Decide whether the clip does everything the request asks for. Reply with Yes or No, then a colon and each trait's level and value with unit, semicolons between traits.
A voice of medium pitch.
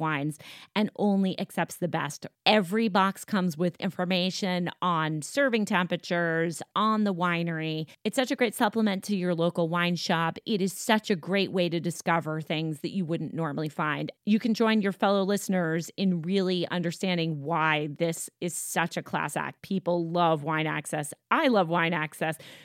Yes: medium, 175 Hz